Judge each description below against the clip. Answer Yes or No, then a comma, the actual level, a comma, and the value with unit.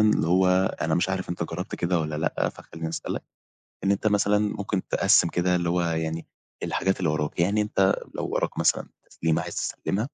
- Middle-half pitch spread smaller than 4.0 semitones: Yes, average, 2.9 semitones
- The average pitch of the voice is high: No, very low, 90 Hz